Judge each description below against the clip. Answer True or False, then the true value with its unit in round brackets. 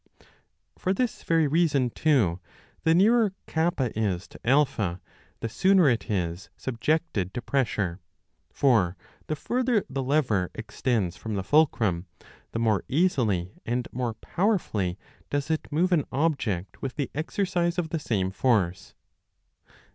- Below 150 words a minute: True (135 wpm)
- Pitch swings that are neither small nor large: False (8.2 semitones)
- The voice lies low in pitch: True (130 Hz)